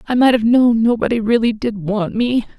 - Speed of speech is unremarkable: No, fast, 210 wpm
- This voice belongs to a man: No, female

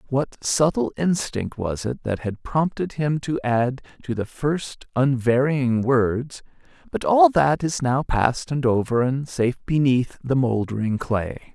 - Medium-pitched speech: No, low, 130 Hz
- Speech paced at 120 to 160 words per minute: Yes, average, 155 wpm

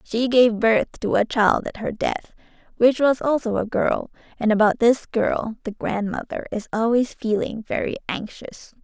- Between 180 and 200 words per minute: No, average, 170 wpm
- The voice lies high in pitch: Yes, high, 225 Hz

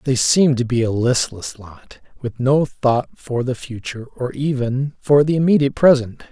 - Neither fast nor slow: Yes, average, 180 wpm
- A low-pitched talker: Yes, low, 130 Hz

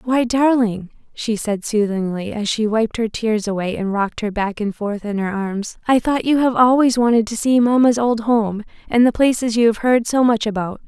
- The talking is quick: Yes, fast, 220 wpm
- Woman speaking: Yes, female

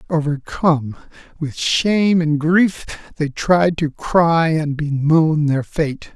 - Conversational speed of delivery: No, slow, 125 wpm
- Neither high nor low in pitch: Yes, medium, 155 Hz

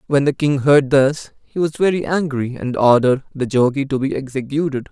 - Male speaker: Yes, male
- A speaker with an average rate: Yes, average, 195 wpm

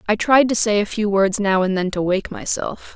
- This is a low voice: No, high, 205 Hz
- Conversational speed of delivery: No, fast, 265 wpm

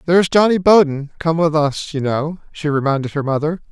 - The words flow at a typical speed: Yes, average, 195 wpm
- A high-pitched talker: No, medium, 155 Hz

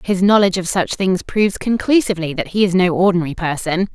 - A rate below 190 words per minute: No, average, 200 wpm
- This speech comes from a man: No, female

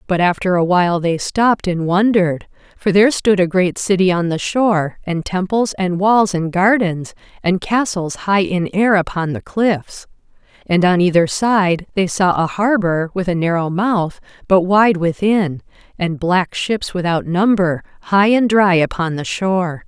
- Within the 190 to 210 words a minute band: No, average, 170 wpm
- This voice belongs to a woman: Yes, female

